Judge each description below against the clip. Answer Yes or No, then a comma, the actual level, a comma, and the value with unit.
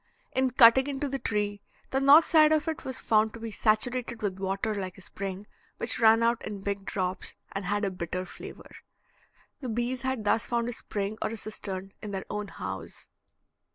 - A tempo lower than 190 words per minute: No, average, 195 wpm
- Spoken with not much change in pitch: No, average, 4.1 semitones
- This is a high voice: Yes, high, 215 Hz